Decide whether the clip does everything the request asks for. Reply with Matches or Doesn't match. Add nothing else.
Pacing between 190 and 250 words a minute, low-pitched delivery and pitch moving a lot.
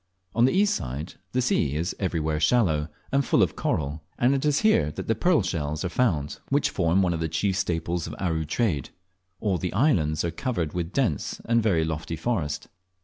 Matches